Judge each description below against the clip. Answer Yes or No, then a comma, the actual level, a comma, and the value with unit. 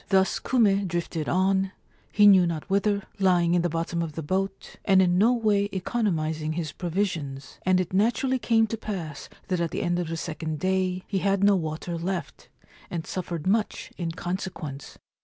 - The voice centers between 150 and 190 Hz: Yes, medium, 185 Hz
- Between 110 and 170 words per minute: No, average, 185 wpm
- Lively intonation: No, average, 3.1 semitones